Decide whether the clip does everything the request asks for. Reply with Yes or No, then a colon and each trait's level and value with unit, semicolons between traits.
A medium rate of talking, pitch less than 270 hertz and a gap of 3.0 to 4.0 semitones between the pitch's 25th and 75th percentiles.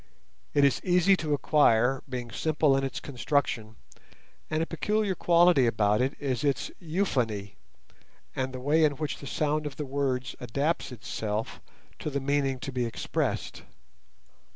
Yes: average, 150 wpm; medium, 140 Hz; average, 3.7 semitones